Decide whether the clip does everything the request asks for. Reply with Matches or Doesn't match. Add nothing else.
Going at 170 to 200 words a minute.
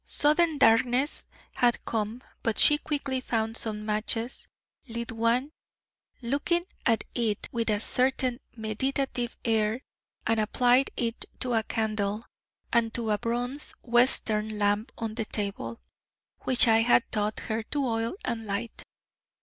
Doesn't match